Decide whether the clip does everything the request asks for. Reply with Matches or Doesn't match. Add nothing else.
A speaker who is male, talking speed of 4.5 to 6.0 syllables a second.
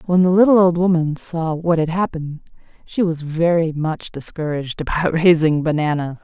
Doesn't match